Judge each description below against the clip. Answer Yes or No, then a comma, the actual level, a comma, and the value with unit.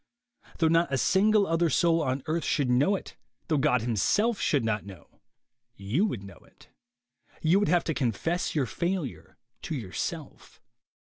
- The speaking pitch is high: No, medium, 155 Hz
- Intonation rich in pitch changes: Yes, wide, 5.9 semitones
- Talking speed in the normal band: Yes, average, 165 wpm